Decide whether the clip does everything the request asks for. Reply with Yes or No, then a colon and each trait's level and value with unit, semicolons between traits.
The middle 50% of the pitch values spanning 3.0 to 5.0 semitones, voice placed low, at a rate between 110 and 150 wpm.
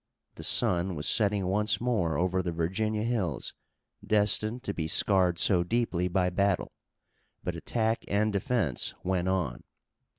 Yes: average, 3.3 semitones; very low, 95 Hz; average, 140 wpm